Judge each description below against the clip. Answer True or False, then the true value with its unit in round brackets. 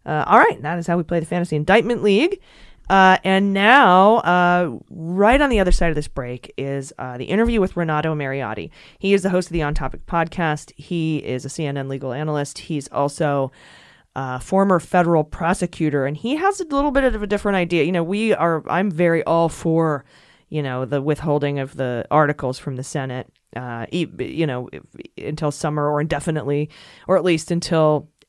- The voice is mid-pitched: True (160 Hz)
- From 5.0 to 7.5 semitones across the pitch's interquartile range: False (4.2 semitones)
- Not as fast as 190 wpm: False (195 wpm)